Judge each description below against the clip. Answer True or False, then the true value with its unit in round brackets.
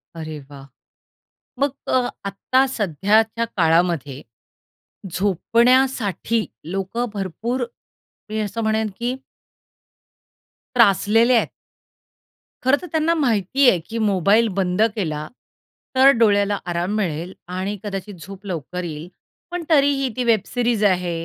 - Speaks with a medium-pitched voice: False (210 Hz)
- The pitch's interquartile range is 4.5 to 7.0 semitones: True (4.9 semitones)